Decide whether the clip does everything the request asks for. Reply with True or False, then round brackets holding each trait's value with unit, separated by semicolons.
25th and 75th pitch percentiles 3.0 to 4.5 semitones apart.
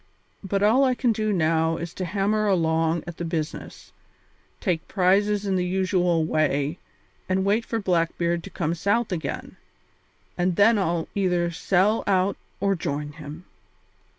True (3.5 semitones)